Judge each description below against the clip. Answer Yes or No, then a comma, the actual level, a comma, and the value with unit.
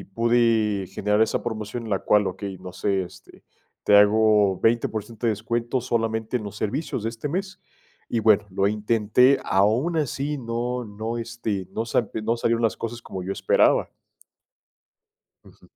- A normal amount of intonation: No, narrow, 2.3 semitones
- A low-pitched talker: Yes, low, 110 Hz